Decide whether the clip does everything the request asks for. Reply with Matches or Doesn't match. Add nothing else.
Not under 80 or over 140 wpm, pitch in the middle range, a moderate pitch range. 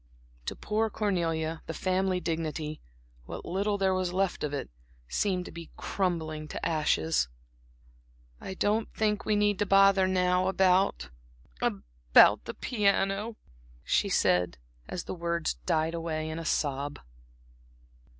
Matches